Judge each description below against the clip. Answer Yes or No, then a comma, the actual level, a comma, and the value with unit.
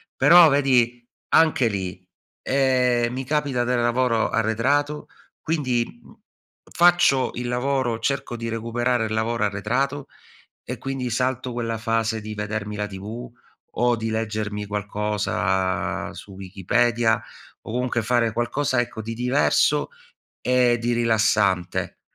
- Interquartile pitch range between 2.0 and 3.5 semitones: Yes, average, 2.7 semitones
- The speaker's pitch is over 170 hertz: No, low, 120 Hz